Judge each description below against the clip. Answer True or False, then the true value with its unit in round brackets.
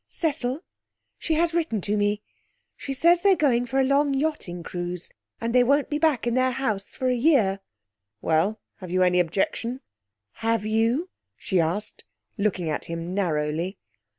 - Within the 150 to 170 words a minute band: True (165 wpm)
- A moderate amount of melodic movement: False (7.0 semitones)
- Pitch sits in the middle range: False (230 Hz)